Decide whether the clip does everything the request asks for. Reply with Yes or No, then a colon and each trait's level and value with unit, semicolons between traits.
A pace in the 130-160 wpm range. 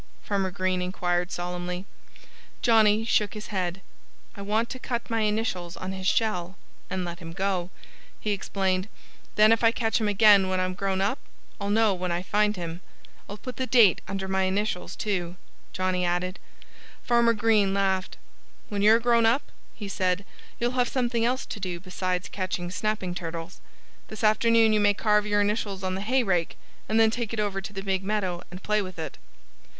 No: average, 185 wpm